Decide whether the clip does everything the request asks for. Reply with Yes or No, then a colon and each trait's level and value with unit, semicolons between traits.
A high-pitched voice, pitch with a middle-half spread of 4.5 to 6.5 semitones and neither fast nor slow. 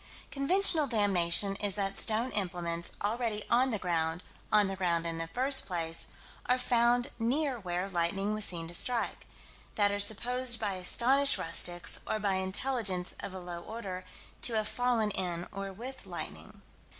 Yes: high, 205 Hz; average, 5.1 semitones; average, 160 wpm